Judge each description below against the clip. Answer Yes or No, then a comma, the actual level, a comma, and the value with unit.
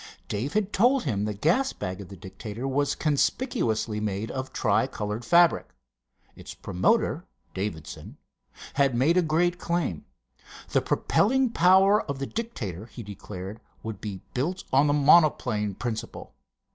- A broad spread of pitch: Yes, wide, 8.7 semitones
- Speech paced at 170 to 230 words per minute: No, average, 145 wpm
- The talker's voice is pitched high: No, low, 130 Hz